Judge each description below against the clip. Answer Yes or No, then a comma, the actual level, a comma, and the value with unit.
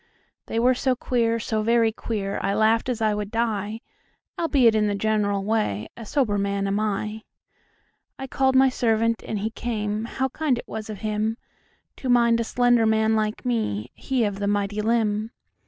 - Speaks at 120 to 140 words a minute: No, average, 155 wpm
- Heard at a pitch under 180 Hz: No, high, 220 Hz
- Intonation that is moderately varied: No, narrow, 2.1 semitones